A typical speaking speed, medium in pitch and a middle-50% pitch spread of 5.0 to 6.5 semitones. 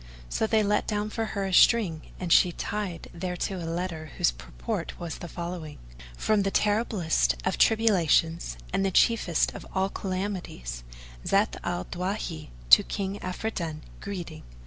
No: average, 150 wpm; medium, 180 Hz; average, 3.9 semitones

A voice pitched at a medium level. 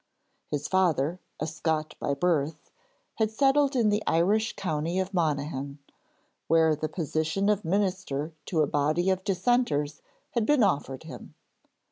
Yes: medium, 165 Hz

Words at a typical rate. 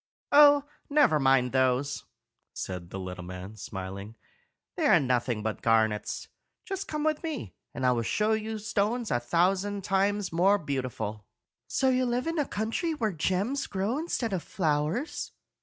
Yes: average, 155 wpm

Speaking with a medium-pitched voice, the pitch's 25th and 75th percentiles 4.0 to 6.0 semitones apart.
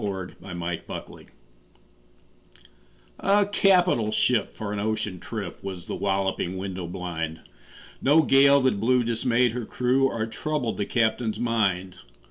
No: low, 110 Hz; average, 4.9 semitones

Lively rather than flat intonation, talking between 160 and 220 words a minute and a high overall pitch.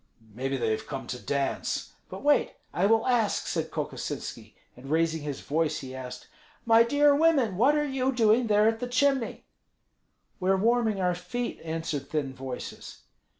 Yes: wide, 8.9 semitones; average, 170 wpm; high, 200 Hz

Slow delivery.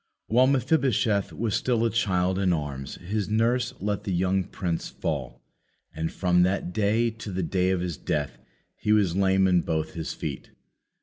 No: average, 175 wpm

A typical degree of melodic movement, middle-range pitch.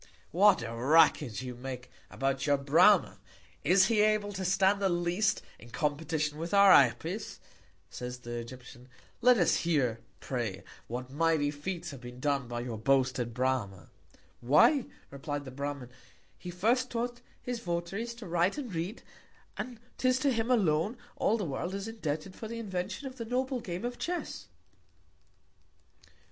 No: wide, 8.0 semitones; medium, 165 Hz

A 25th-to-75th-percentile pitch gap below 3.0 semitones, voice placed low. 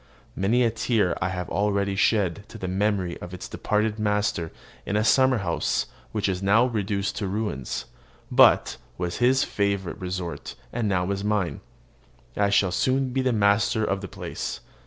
Yes: narrow, 2.6 semitones; low, 100 Hz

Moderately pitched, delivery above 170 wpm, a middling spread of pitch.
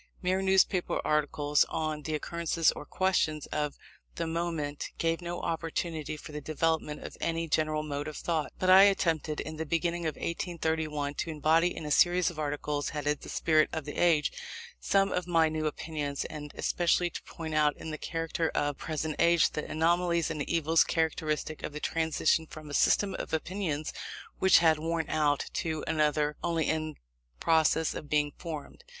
No: medium, 160 Hz; average, 180 wpm; narrow, 1.8 semitones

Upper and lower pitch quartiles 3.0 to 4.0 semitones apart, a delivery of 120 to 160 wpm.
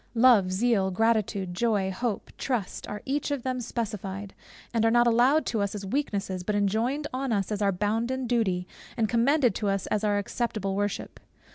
No: average, 3.5 semitones; average, 180 wpm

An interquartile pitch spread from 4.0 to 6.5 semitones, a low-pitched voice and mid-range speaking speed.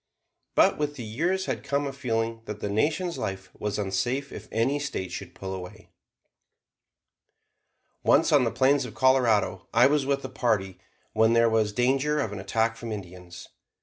Yes: average, 5.2 semitones; low, 115 Hz; average, 175 wpm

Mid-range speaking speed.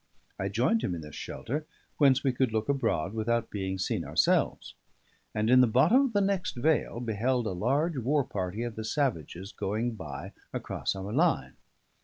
Yes: average, 180 wpm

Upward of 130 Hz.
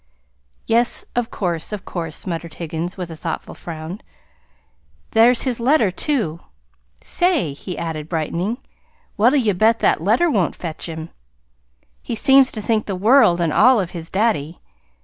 Yes: high, 190 Hz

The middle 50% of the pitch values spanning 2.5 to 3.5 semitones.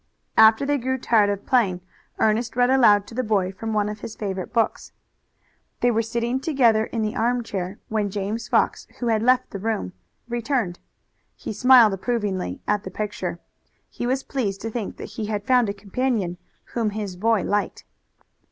Yes: average, 2.9 semitones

